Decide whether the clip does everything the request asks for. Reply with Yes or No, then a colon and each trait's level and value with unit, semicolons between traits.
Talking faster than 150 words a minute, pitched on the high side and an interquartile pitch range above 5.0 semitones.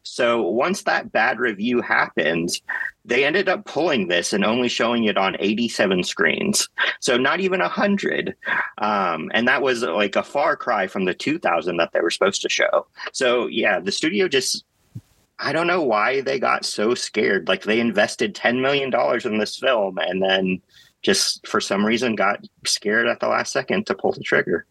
No: average, 185 wpm; low, 115 Hz; wide, 5.4 semitones